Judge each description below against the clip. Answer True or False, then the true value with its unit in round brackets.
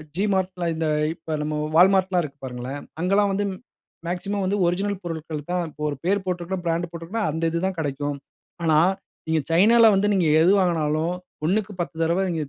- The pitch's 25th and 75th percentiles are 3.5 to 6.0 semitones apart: False (3.1 semitones)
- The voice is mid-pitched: True (175 Hz)